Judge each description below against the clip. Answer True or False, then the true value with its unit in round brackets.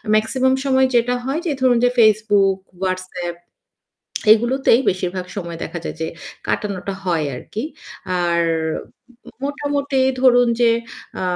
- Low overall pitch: False (215 Hz)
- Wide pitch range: True (6.0 semitones)